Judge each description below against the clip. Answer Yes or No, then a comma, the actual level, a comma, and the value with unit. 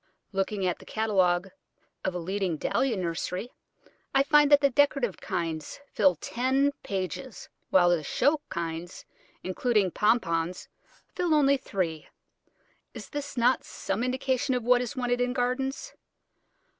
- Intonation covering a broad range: Yes, wide, 6.4 semitones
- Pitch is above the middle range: Yes, high, 220 Hz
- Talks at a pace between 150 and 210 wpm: No, slow, 135 wpm